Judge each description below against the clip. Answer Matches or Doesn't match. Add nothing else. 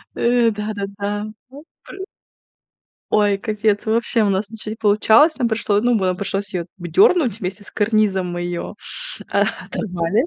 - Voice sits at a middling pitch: Doesn't match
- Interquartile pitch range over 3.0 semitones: Doesn't match